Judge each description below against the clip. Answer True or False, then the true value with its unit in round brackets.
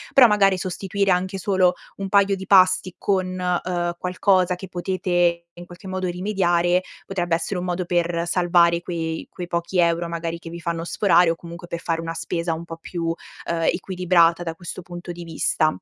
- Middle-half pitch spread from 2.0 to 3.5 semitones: False (1.6 semitones)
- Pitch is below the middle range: False (175 Hz)